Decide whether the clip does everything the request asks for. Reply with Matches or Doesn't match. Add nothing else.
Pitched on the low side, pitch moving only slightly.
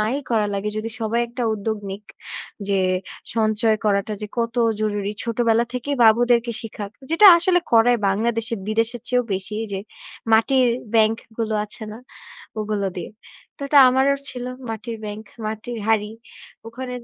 Doesn't match